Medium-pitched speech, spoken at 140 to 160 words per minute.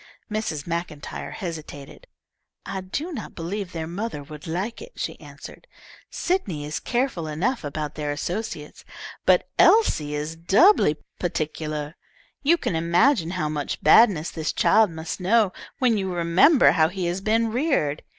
Yes: medium, 175 Hz; average, 145 wpm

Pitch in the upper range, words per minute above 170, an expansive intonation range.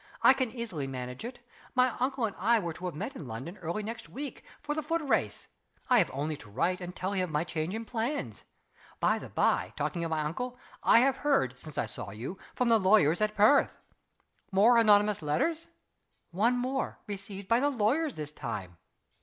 Yes: high, 205 Hz; fast, 205 wpm; wide, 7.7 semitones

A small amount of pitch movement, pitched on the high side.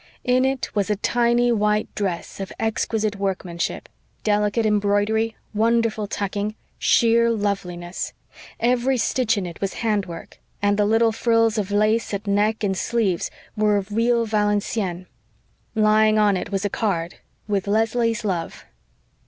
Yes: narrow, 2.1 semitones; high, 210 Hz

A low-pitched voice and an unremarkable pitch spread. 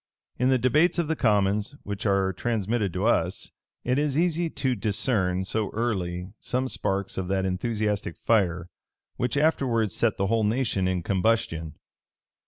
Yes: low, 105 Hz; average, 4.5 semitones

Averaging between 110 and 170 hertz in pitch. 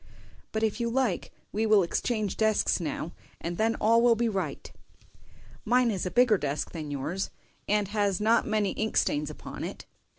No: high, 210 Hz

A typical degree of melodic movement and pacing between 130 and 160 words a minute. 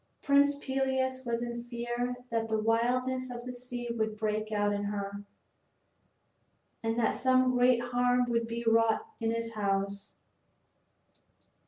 No: narrow, 2.1 semitones; average, 140 wpm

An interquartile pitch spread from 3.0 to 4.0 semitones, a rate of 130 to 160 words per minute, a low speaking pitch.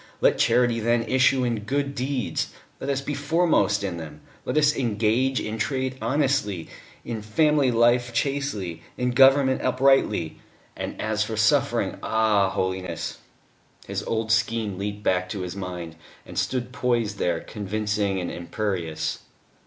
No: average, 4.7 semitones; average, 145 wpm; low, 110 Hz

